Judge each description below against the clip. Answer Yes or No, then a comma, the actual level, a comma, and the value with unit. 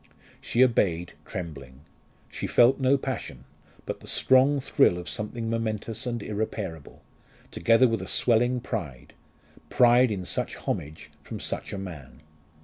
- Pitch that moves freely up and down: Yes, wide, 5.8 semitones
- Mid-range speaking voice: No, low, 110 Hz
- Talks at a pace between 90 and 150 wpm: Yes, average, 140 wpm